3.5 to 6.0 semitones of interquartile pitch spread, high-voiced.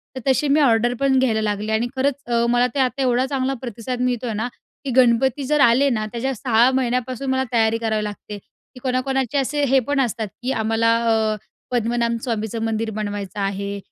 No: average, 3.0 semitones; high, 240 Hz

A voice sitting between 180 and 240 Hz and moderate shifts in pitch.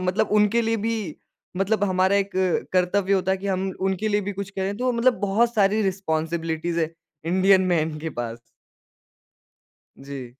Yes: high, 190 Hz; average, 3.2 semitones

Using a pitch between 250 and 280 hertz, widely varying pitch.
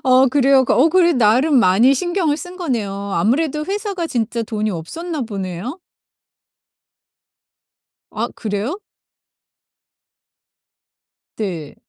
Yes: very high, 260 Hz; wide, 7.3 semitones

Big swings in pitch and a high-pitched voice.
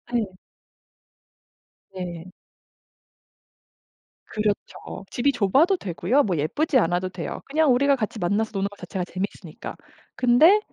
Yes: wide, 6.6 semitones; high, 205 Hz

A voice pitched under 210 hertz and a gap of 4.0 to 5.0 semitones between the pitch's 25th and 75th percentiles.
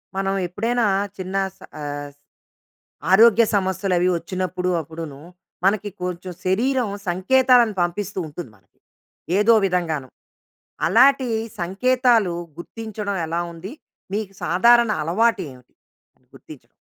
Yes: high, 190 Hz; average, 4.7 semitones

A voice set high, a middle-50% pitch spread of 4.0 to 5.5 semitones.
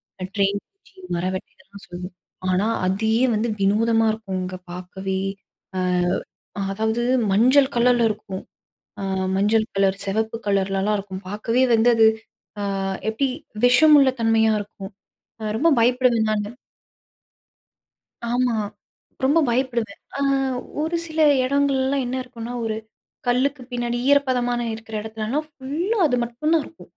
Yes: high, 225 Hz; average, 4.3 semitones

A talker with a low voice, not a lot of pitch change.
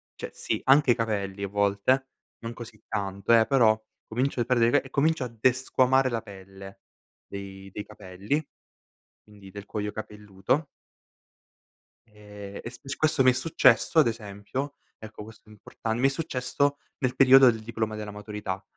No: low, 110 Hz; average, 4.2 semitones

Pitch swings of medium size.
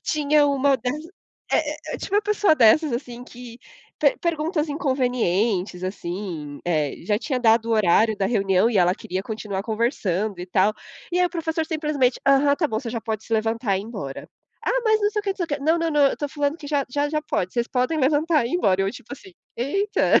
No: wide, 6.4 semitones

